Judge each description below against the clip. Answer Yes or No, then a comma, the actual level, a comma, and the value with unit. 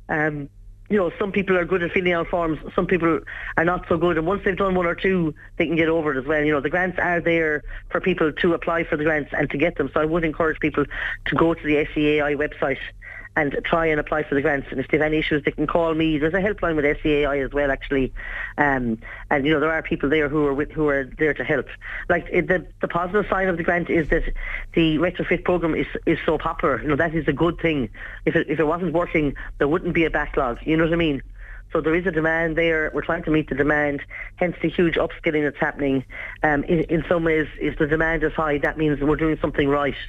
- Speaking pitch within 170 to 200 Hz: No, medium, 160 Hz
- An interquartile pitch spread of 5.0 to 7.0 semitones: No, narrow, 2.4 semitones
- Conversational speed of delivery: No, fast, 260 wpm